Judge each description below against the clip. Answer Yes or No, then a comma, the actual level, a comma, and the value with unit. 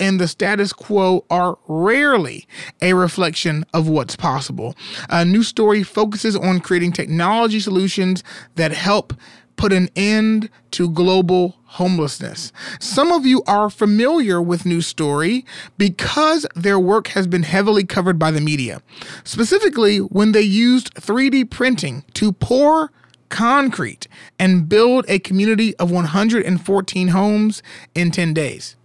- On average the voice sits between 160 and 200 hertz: Yes, high, 190 Hz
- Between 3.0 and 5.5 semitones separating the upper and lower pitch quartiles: Yes, average, 3.5 semitones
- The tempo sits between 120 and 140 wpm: Yes, slow, 135 wpm